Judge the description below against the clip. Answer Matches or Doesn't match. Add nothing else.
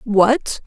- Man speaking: Doesn't match